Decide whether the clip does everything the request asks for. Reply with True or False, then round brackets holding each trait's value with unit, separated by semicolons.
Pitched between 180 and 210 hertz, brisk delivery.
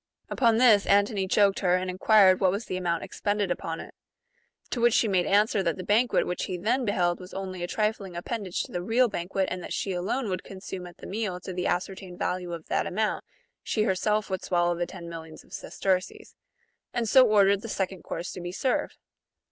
True (190 Hz; 220 wpm)